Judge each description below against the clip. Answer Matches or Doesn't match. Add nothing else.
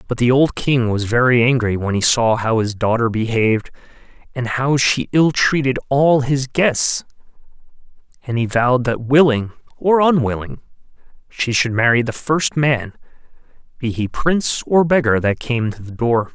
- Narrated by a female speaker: Doesn't match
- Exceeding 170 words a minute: Doesn't match